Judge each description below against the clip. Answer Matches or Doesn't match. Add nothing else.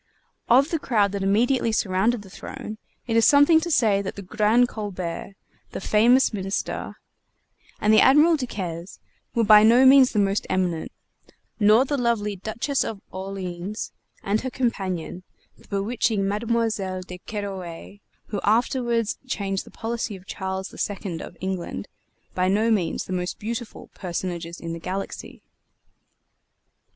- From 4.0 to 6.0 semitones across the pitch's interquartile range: Doesn't match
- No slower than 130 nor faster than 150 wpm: Matches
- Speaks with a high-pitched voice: Matches